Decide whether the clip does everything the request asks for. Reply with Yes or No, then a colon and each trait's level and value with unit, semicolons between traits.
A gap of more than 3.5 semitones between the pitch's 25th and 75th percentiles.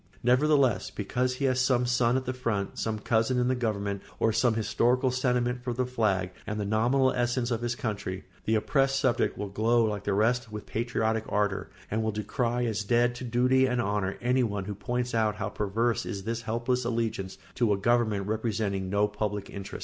No: average, 2.9 semitones